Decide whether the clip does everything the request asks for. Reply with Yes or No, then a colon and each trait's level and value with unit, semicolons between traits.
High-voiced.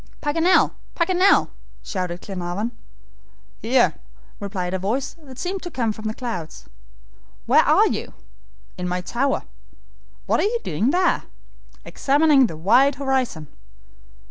Yes: high, 245 Hz